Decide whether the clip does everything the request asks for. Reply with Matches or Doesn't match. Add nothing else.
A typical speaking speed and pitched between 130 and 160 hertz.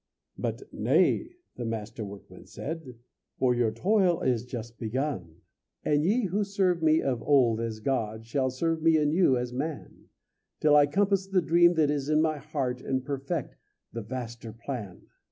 Matches